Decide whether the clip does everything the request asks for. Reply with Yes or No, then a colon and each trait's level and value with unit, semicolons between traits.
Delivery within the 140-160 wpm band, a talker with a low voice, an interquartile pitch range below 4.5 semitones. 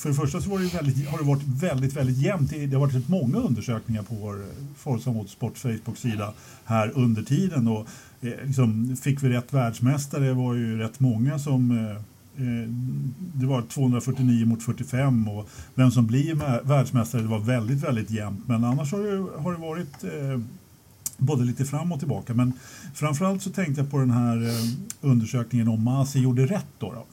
No: average, 190 wpm; low, 130 Hz; average, 3.1 semitones